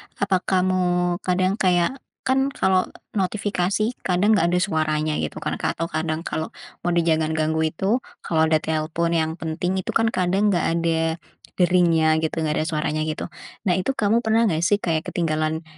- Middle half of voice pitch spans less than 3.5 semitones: Yes, average, 3.0 semitones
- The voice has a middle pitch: Yes, medium, 170 Hz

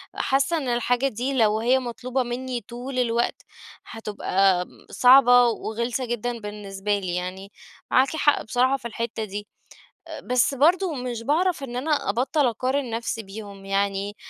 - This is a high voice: Yes, high, 240 Hz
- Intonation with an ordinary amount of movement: Yes, average, 3.8 semitones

